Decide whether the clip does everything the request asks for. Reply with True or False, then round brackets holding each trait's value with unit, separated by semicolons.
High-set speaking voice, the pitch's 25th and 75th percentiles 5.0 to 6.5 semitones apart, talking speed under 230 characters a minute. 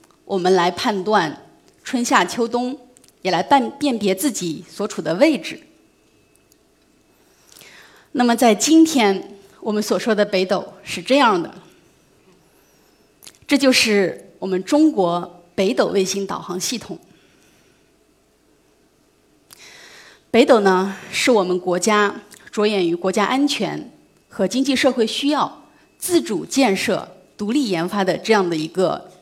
True (205 Hz; 5.3 semitones; 180 characters per minute)